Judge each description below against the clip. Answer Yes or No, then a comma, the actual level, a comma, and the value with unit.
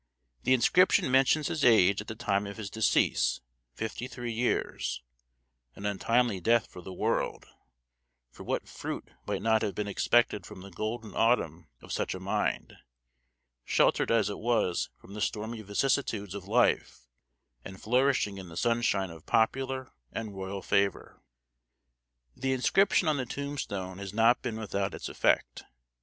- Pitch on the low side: Yes, low, 110 Hz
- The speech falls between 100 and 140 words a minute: No, average, 155 wpm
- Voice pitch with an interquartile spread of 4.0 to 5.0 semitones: No, average, 3.6 semitones